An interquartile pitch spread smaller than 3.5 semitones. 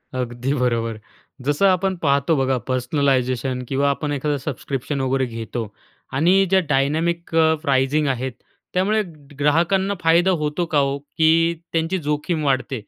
No: average, 3.8 semitones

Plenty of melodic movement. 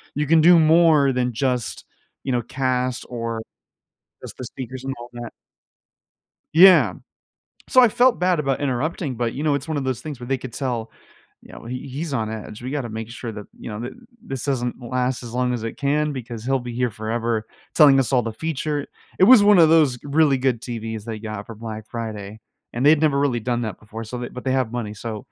No: average, 3.8 semitones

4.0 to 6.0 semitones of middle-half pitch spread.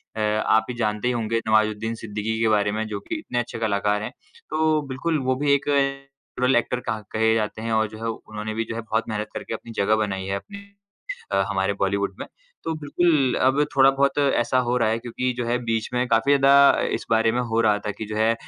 No: average, 3.5 semitones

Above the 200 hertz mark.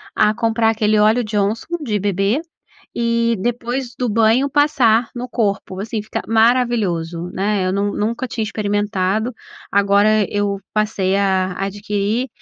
Yes: high, 215 Hz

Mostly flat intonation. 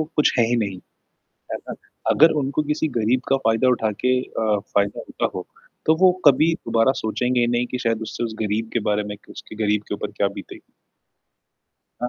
No: average, 3.1 semitones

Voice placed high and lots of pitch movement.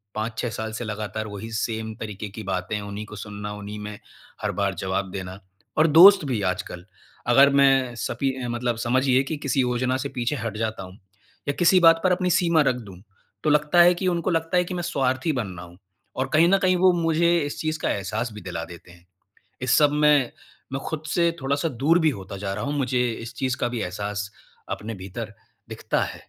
No: low, 125 Hz; wide, 6.4 semitones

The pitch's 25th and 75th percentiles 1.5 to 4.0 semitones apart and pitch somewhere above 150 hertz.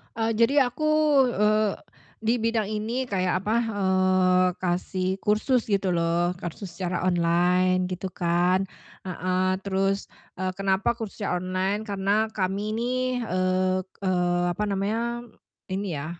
Yes: average, 2.9 semitones; high, 190 Hz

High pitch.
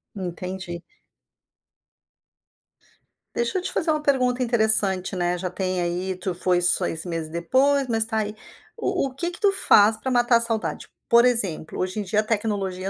Yes: high, 210 Hz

